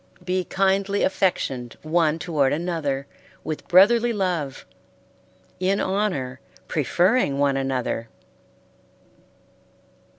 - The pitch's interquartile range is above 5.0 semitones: Yes, wide, 5.6 semitones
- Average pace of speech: No, slow, 80 wpm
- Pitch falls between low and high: Yes, medium, 170 Hz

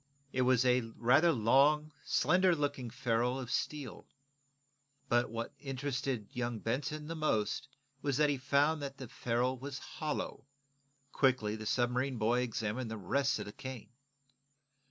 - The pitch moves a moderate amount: Yes, average, 3.0 semitones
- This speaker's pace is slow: No, average, 145 wpm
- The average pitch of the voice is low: Yes, low, 130 Hz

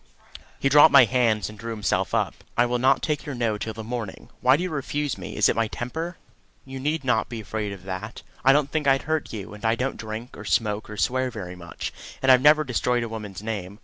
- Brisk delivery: Yes, fast, 245 wpm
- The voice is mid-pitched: No, low, 120 Hz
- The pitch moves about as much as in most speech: Yes, average, 4.0 semitones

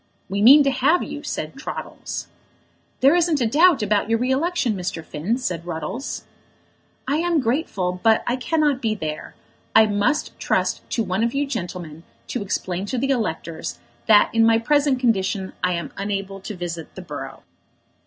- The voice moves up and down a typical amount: No, wide, 6.8 semitones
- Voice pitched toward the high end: Yes, high, 220 Hz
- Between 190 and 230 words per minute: No, average, 175 wpm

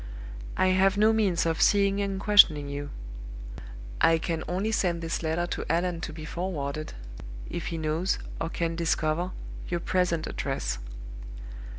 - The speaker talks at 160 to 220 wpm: No, average, 150 wpm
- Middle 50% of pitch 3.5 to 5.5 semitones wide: No, average, 2.9 semitones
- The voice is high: No, medium, 170 Hz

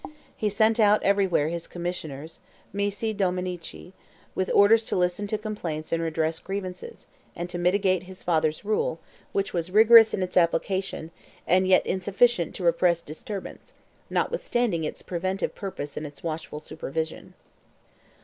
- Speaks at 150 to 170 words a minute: No, average, 140 wpm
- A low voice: No, medium, 185 Hz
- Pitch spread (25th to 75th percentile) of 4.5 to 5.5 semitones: No, average, 3.4 semitones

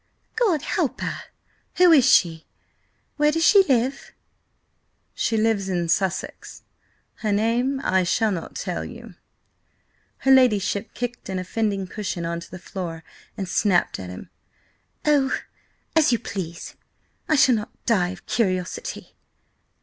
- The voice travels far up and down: Yes, wide, 6.2 semitones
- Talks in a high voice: Yes, high, 210 Hz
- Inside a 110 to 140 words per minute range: Yes, slow, 135 wpm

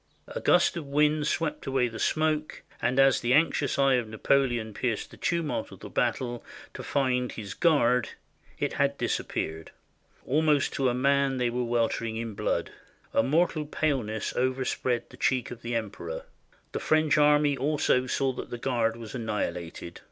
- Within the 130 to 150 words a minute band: No, average, 165 wpm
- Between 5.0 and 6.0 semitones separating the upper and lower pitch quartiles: No, average, 3.9 semitones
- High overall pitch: No, low, 130 Hz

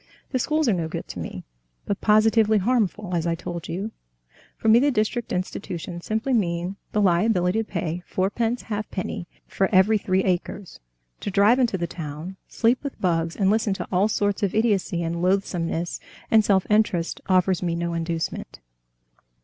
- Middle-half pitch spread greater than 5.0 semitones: No, average, 4.0 semitones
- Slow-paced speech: No, average, 170 wpm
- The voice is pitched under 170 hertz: No, high, 195 Hz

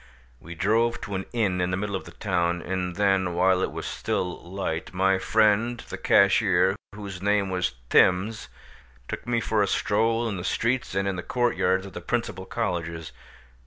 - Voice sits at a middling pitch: No, very low, 95 Hz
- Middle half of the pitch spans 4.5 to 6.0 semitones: No, average, 3.0 semitones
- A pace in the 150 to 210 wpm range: Yes, average, 190 wpm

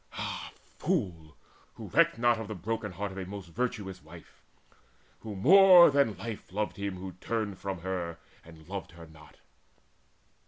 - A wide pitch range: No, average, 3.9 semitones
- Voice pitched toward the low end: Yes, low, 100 Hz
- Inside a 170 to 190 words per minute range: No, average, 160 wpm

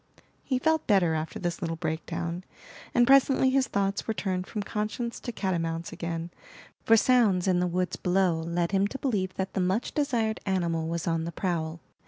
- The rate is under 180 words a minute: No, average, 185 wpm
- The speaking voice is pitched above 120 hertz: Yes, medium, 185 Hz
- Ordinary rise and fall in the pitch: Yes, average, 4.5 semitones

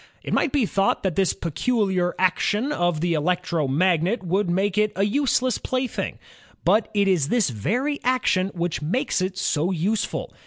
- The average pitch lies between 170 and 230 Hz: Yes, high, 190 Hz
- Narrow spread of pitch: No, average, 4.3 semitones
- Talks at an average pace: Yes, average, 160 wpm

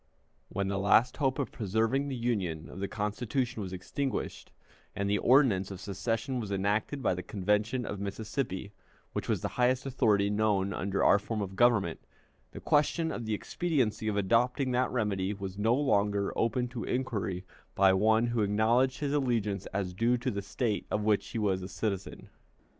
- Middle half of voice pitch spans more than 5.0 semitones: No, average, 3.8 semitones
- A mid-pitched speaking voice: No, low, 105 Hz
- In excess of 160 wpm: Yes, average, 180 wpm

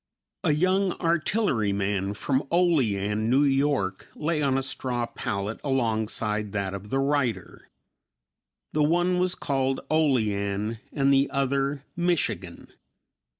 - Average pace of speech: No, slow, 115 wpm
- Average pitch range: No, wide, 6.1 semitones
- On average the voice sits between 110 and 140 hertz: Yes, low, 135 Hz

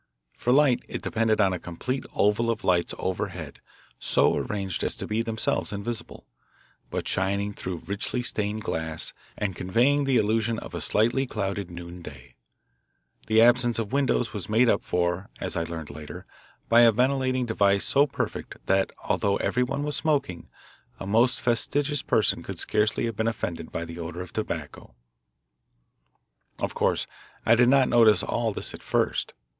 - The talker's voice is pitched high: No, low, 110 Hz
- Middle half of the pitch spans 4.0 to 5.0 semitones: Yes, average, 4.5 semitones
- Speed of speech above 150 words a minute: Yes, average, 160 wpm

